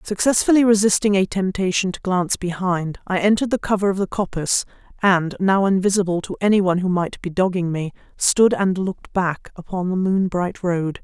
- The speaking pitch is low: No, high, 190 Hz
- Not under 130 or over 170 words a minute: No, average, 185 wpm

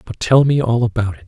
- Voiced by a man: Yes, male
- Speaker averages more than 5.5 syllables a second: Yes, 6.0 syllables/s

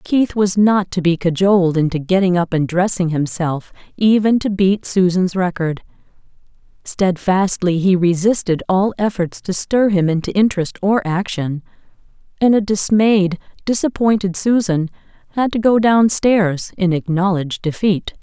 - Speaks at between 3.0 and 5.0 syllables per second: Yes, 4.5 syllables/s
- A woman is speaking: Yes, female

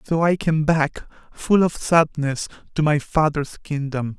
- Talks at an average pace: Yes, average, 160 wpm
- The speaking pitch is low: No, medium, 150 Hz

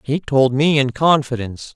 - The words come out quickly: No, average, 170 wpm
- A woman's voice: No, male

